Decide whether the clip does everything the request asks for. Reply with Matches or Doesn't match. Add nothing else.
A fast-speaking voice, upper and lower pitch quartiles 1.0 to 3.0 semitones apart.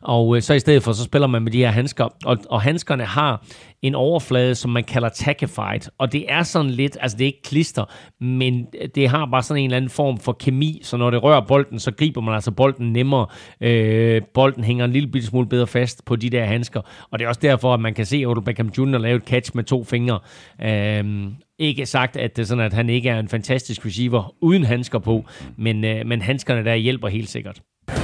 Matches